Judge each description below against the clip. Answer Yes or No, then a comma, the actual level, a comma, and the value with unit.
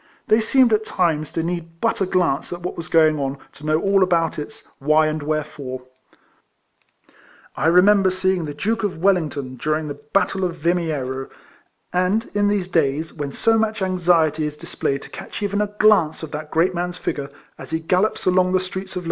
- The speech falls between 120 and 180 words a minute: No, average, 195 wpm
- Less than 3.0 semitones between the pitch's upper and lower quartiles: No, average, 3.6 semitones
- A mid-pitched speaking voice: Yes, medium, 170 Hz